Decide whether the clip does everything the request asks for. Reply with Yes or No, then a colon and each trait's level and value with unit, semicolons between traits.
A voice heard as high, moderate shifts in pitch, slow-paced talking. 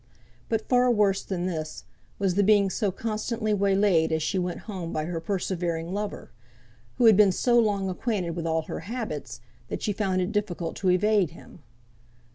No: high, 195 Hz; average, 3.3 semitones; average, 180 wpm